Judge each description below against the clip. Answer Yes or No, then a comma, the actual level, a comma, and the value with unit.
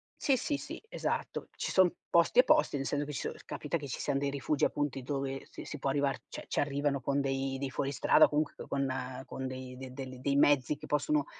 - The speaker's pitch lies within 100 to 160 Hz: Yes, medium, 140 Hz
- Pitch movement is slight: Yes, narrow, 1.8 semitones